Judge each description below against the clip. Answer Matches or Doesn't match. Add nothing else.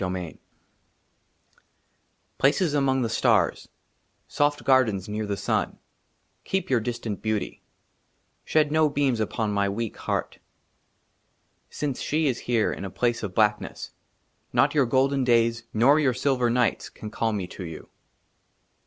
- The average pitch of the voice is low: Matches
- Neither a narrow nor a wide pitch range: Matches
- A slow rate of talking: Doesn't match